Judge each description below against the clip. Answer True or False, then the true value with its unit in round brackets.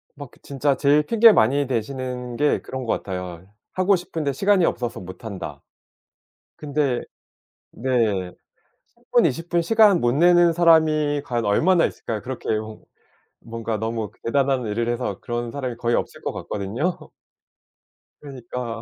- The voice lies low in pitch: True (130 Hz)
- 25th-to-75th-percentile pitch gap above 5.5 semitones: False (5.2 semitones)